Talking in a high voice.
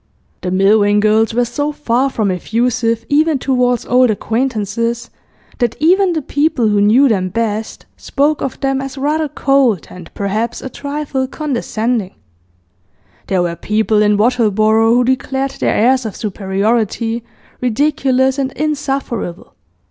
Yes: high, 240 Hz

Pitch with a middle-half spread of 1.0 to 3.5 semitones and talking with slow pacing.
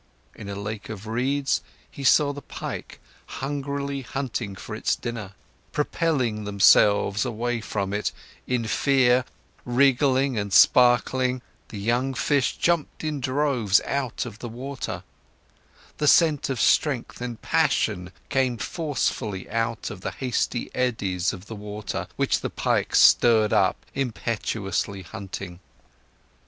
No: average, 4.5 semitones; slow, 130 wpm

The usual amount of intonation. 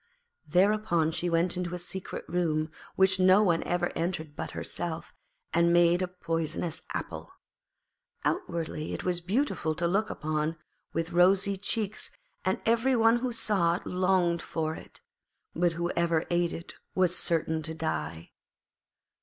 No: narrow, 2.3 semitones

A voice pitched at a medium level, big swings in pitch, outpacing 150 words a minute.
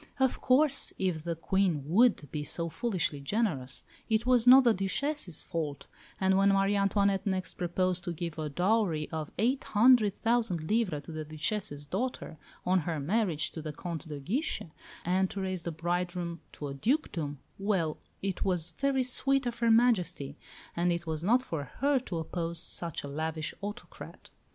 Yes: medium, 180 Hz; wide, 5.8 semitones; average, 175 wpm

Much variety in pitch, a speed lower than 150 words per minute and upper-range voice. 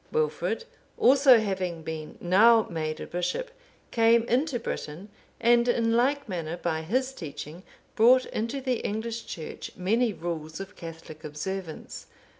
Yes: wide, 6.5 semitones; slow, 135 wpm; high, 210 Hz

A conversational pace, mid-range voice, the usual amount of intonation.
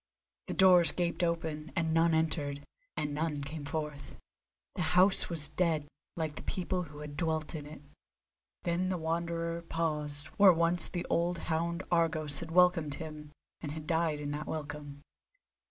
No: average, 160 wpm; medium, 160 Hz; narrow, 2.2 semitones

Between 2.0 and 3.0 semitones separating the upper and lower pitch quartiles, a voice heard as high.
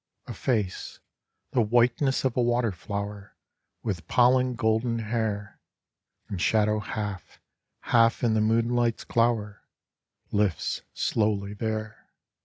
No: narrow, 2.4 semitones; low, 110 Hz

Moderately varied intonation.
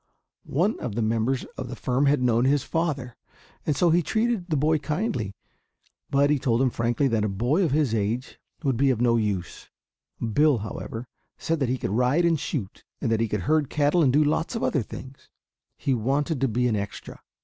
Yes: average, 4.7 semitones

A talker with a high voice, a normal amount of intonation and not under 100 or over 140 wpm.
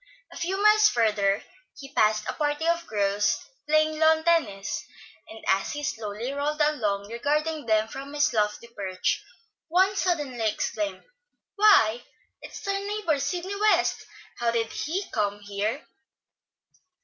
No: very high, 280 Hz; wide, 7.8 semitones; slow, 135 wpm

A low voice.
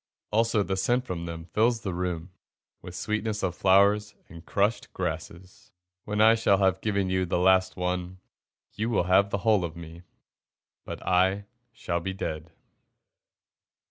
Yes: very low, 95 Hz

